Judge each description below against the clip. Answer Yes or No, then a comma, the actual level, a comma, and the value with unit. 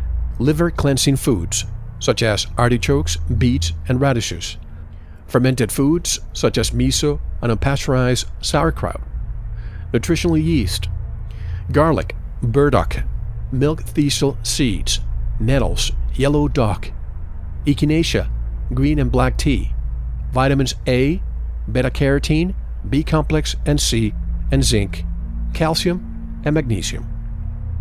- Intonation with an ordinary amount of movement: No, wide, 8.1 semitones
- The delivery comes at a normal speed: No, slow, 95 wpm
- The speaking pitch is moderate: No, low, 115 Hz